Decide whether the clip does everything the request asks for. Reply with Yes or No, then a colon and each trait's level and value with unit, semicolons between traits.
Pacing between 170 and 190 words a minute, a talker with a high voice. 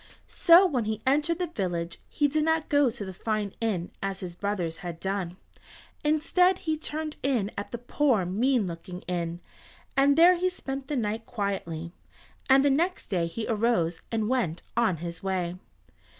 Yes: average, 175 wpm; high, 220 Hz